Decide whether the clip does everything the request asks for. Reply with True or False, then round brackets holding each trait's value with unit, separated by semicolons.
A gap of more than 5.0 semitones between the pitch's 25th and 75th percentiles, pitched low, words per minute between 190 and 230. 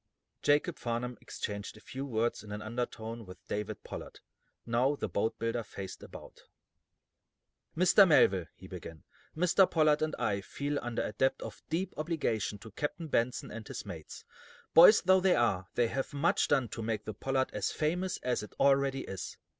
False (5.6 semitones; 120 Hz; 175 wpm)